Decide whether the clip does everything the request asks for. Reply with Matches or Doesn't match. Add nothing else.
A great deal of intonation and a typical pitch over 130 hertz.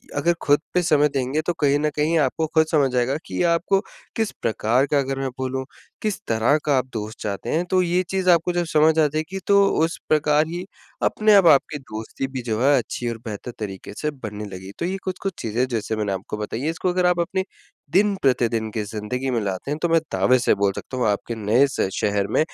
Matches